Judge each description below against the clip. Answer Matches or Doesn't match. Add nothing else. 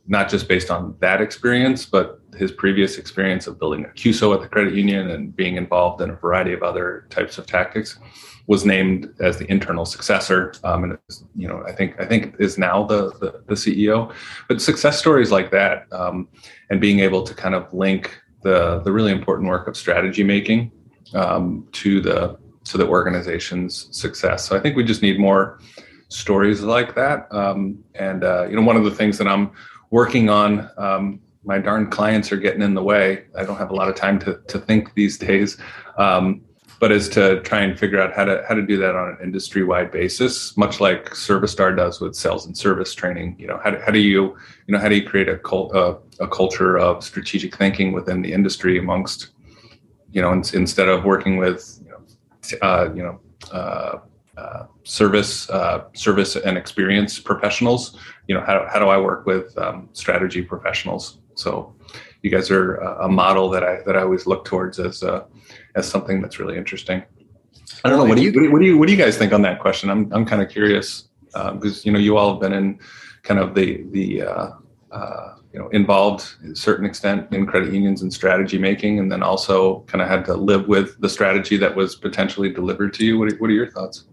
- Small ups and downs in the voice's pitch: Matches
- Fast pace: Matches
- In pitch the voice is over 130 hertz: Doesn't match